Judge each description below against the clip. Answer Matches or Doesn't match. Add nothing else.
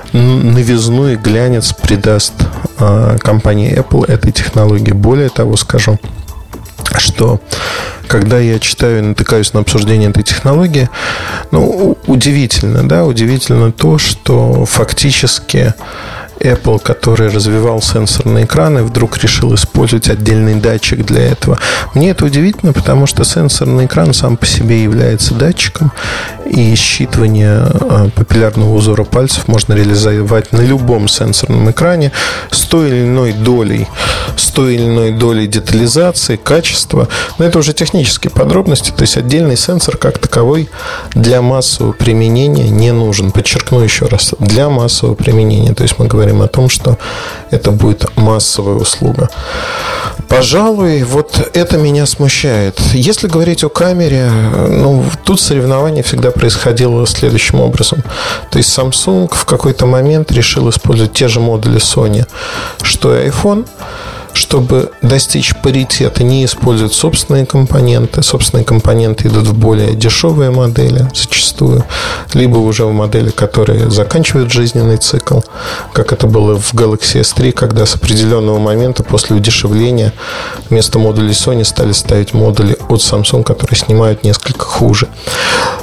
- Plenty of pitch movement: Doesn't match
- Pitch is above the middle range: Doesn't match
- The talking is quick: Doesn't match